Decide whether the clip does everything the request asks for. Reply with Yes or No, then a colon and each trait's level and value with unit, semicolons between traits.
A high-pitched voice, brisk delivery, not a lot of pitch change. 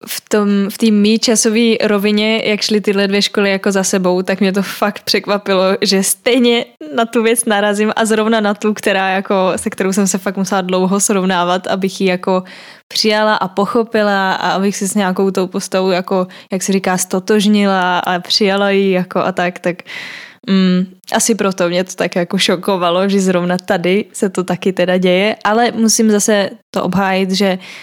Yes: high, 195 Hz; fast, 185 wpm; narrow, 2.1 semitones